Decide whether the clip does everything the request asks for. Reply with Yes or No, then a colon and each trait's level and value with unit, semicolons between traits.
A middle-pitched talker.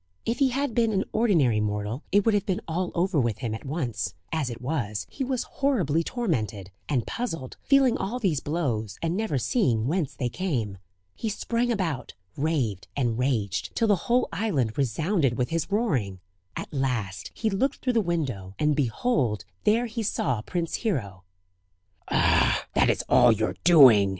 Yes: medium, 150 Hz